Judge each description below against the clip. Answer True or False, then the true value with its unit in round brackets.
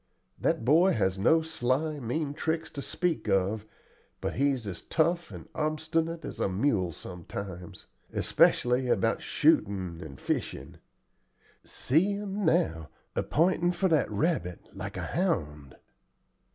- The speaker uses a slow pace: True (130 wpm)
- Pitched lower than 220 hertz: True (140 Hz)